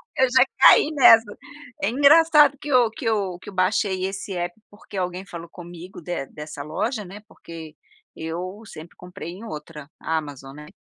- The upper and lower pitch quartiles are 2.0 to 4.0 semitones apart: No, average, 5.3 semitones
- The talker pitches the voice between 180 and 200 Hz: Yes, medium, 185 Hz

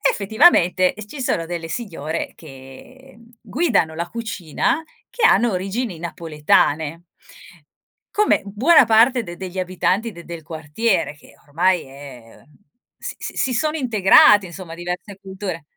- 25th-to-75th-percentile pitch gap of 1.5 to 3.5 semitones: No, wide, 5.9 semitones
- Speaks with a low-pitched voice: No, medium, 185 Hz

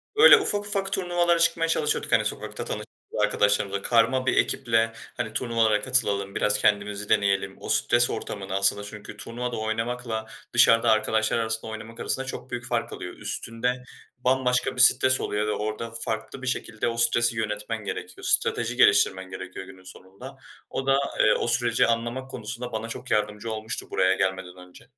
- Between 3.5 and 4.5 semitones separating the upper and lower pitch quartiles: No, average, 3.1 semitones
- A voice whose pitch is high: No, low, 115 Hz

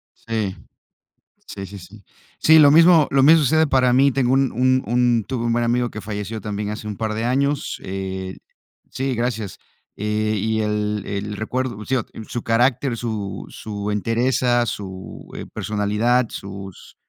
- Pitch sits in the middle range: No, low, 115 Hz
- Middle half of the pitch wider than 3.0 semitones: Yes, average, 3.6 semitones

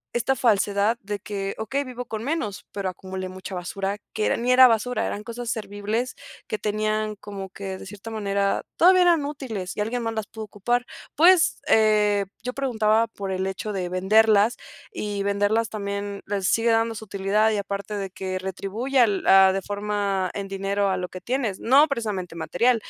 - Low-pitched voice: No, high, 210 Hz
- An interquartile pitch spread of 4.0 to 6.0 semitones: No, average, 2.7 semitones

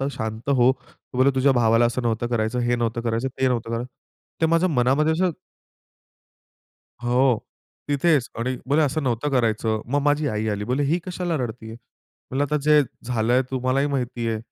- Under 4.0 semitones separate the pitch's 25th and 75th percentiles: Yes, average, 3.4 semitones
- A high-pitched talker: No, low, 125 Hz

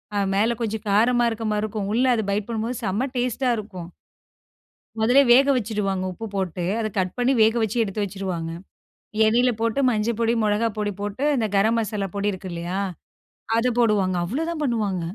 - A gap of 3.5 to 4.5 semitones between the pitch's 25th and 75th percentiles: No, average, 2.9 semitones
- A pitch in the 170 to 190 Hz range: No, high, 215 Hz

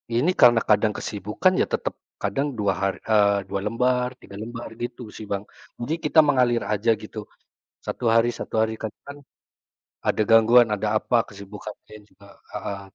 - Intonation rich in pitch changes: No, average, 2.9 semitones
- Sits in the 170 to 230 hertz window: No, low, 110 Hz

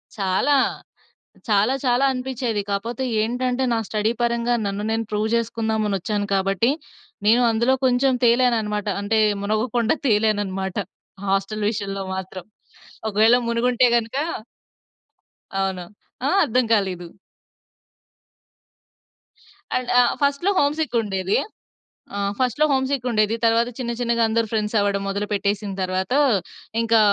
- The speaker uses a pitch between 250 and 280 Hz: No, high, 220 Hz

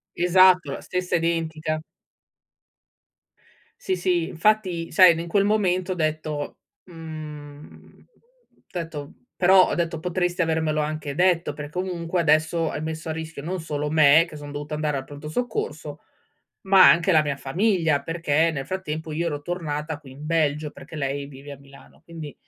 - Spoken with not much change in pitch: No, average, 3.0 semitones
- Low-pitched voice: No, medium, 160 Hz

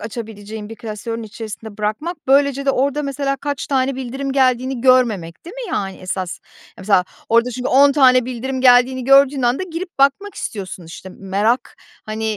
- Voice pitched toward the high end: Yes, very high, 250 Hz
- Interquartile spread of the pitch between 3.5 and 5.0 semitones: Yes, average, 4.2 semitones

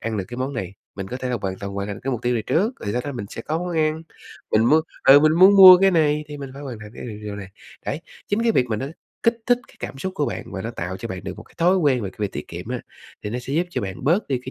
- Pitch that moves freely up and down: Yes, wide, 7.0 semitones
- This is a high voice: No, low, 130 Hz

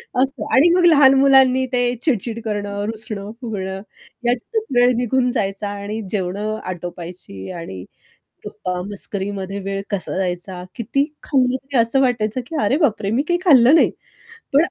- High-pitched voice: Yes, high, 220 Hz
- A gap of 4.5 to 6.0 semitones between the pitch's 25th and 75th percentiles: Yes, average, 4.9 semitones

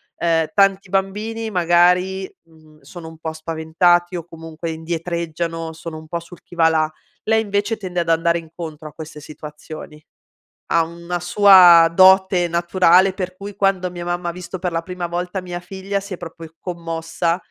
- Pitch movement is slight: Yes, narrow, 2.3 semitones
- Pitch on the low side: No, medium, 175 Hz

